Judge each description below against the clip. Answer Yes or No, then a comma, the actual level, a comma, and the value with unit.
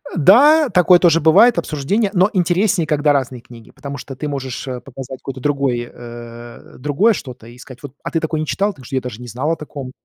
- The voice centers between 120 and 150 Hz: Yes, medium, 140 Hz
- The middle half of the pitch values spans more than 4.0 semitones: Yes, average, 5.3 semitones